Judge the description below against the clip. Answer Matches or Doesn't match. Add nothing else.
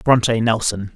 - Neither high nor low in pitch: Doesn't match